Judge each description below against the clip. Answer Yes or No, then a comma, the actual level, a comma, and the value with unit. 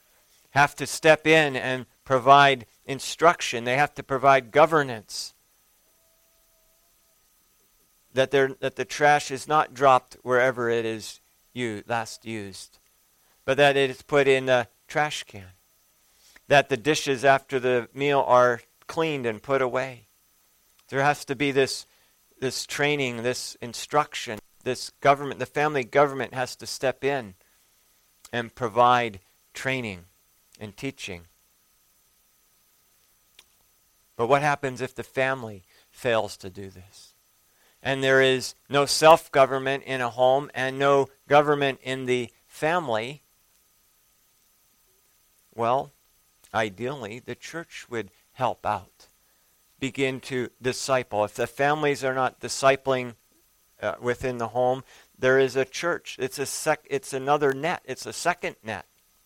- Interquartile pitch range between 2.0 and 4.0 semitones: Yes, average, 2.8 semitones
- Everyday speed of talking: No, slow, 130 wpm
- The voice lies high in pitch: No, low, 130 Hz